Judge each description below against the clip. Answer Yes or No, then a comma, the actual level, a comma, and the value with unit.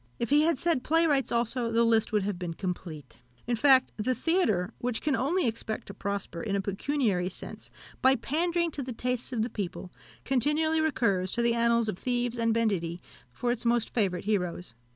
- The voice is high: Yes, high, 235 Hz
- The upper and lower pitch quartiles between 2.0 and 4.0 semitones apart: No, average, 5.0 semitones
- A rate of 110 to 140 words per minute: No, average, 195 wpm